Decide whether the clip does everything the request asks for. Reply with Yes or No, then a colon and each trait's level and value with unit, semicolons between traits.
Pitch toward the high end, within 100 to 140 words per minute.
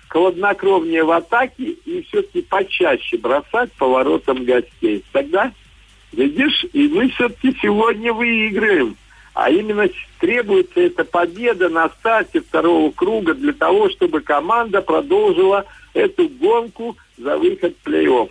Yes: high, 245 Hz; average, 120 wpm